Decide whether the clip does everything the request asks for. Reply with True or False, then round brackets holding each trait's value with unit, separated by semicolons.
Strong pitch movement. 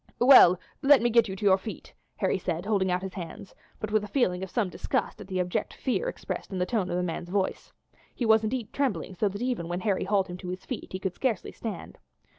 False (3.7 semitones)